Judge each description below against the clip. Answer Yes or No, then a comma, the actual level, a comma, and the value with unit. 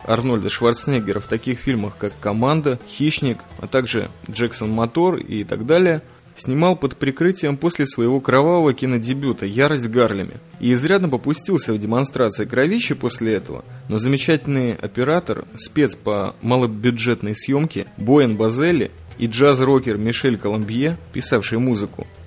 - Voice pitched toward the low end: Yes, low, 125 Hz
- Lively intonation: No, average, 4.3 semitones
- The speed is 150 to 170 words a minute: No, average, 125 wpm